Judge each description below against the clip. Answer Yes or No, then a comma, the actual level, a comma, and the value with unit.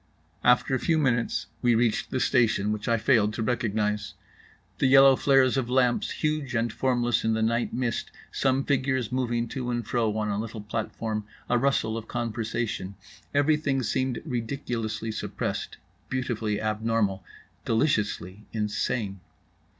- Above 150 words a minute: No, average, 140 wpm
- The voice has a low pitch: Yes, low, 120 Hz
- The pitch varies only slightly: No, average, 3.1 semitones